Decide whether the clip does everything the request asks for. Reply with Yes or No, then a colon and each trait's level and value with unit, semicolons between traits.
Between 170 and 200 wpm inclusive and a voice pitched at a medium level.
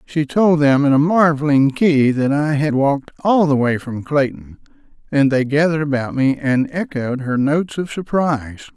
Yes: average, 185 wpm; medium, 145 Hz